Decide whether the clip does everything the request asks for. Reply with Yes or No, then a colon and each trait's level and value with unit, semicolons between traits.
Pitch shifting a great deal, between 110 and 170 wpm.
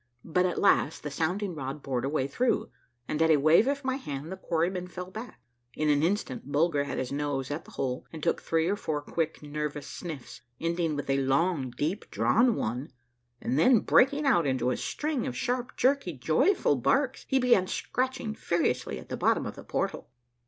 No: wide, 6.4 semitones; average, 200 wpm